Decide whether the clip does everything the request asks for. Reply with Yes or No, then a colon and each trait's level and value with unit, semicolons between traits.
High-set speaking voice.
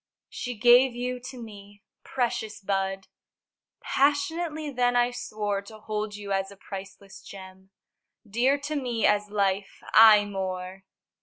Yes: high, 210 Hz